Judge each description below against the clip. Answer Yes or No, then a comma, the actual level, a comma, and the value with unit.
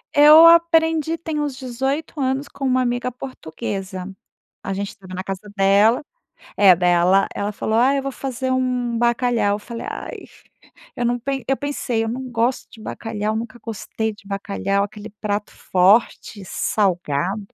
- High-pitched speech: Yes, high, 230 Hz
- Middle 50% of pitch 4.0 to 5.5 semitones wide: Yes, average, 4.7 semitones